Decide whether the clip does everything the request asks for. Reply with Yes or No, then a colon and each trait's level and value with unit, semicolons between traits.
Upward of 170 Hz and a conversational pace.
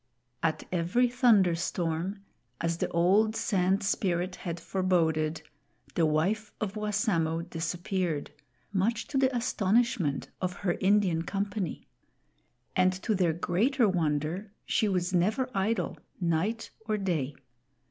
No: medium, 185 Hz; slow, 115 wpm